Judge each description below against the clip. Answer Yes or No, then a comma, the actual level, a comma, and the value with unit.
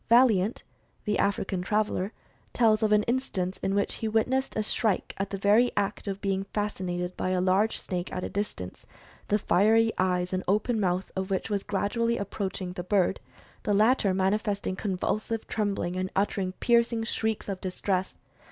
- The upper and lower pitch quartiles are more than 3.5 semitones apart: No, narrow, 2.6 semitones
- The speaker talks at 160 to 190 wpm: Yes, average, 170 wpm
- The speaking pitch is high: Yes, high, 200 Hz